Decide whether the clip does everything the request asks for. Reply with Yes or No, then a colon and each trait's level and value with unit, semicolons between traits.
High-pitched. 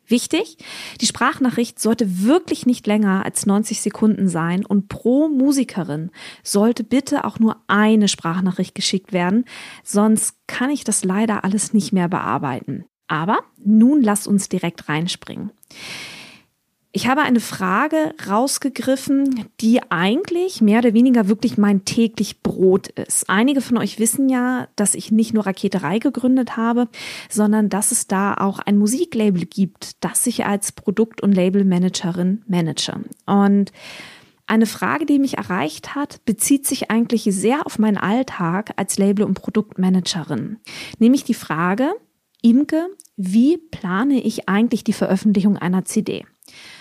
Yes: high, 215 Hz